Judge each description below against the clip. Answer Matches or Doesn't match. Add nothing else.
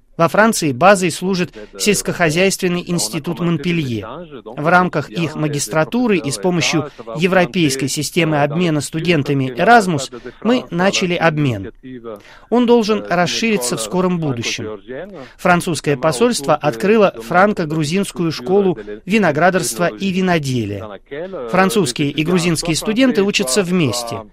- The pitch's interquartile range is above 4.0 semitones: Matches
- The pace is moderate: Doesn't match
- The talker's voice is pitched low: Doesn't match